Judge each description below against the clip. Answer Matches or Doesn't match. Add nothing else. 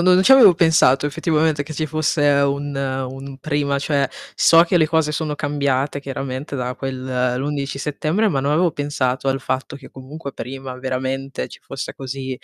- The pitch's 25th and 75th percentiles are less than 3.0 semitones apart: Matches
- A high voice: Doesn't match